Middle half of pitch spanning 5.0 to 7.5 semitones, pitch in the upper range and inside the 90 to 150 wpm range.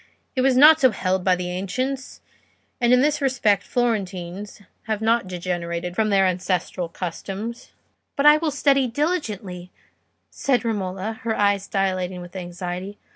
Yes: average, 5.3 semitones; high, 200 Hz; average, 145 wpm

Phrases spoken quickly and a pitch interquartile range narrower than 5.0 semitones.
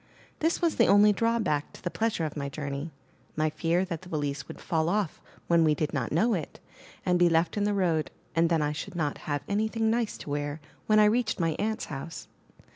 No: fast, 225 wpm; wide, 5.4 semitones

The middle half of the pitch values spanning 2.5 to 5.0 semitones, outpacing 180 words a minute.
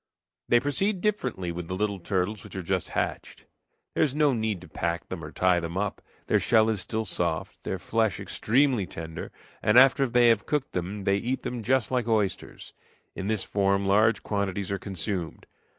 Yes: average, 4.3 semitones; average, 190 wpm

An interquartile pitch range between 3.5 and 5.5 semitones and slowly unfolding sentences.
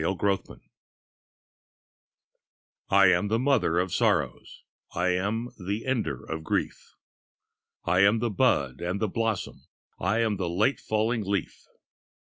Yes: average, 3.9 semitones; slow, 130 wpm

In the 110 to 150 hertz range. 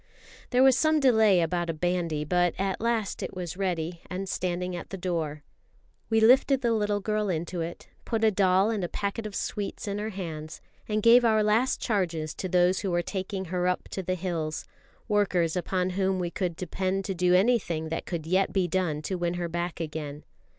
No: medium, 185 Hz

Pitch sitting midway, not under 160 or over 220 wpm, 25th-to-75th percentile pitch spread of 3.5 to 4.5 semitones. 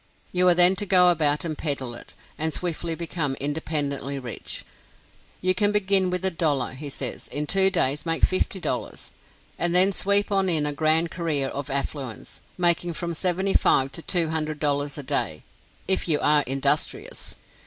Yes: medium, 160 Hz; average, 165 wpm; average, 3.9 semitones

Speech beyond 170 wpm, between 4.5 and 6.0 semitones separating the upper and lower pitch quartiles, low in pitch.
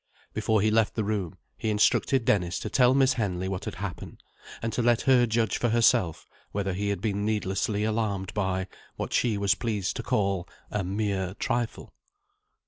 No: average, 180 wpm; average, 2.8 semitones; low, 105 Hz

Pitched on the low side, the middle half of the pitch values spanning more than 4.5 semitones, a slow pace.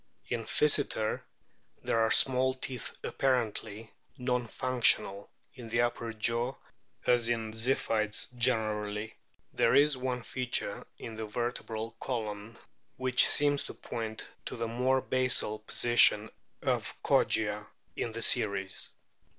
No: low, 115 Hz; narrow, 2.6 semitones; slow, 125 wpm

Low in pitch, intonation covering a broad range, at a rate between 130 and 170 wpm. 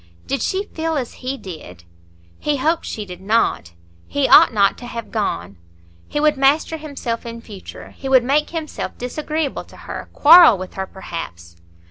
No: very high, 250 Hz; wide, 7.3 semitones; average, 165 wpm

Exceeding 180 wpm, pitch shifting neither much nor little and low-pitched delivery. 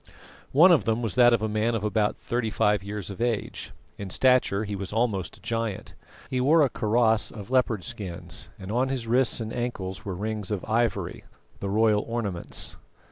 Yes: average, 190 wpm; average, 3.0 semitones; low, 110 Hz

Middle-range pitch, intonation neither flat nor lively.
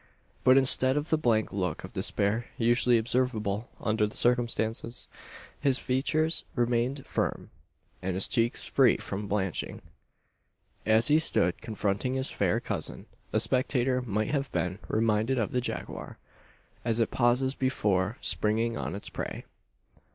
No: low, 120 Hz; average, 3.4 semitones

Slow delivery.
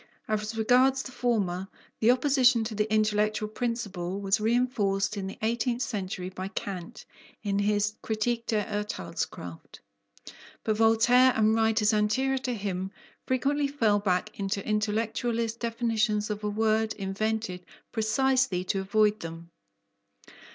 Yes: slow, 130 wpm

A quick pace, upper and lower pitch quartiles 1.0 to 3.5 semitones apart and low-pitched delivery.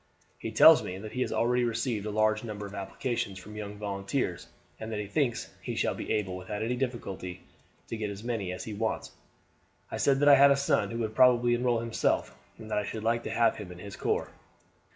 Yes: fast, 230 wpm; average, 2.9 semitones; low, 110 Hz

